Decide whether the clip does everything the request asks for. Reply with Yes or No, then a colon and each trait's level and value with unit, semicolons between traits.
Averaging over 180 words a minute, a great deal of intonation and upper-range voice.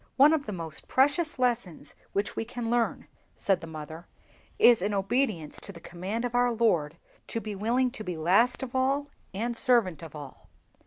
Yes: average, 190 wpm; wide, 6.0 semitones; high, 220 Hz